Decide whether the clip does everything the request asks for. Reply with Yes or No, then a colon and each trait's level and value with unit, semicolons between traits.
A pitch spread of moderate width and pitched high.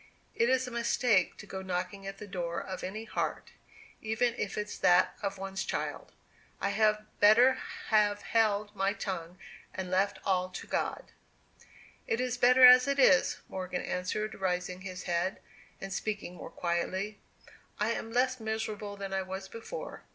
Yes: average, 3.1 semitones; high, 200 Hz